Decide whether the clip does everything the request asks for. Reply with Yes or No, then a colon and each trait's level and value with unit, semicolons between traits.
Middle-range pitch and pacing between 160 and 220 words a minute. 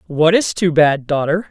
Yes: medium, 160 Hz; average, 200 wpm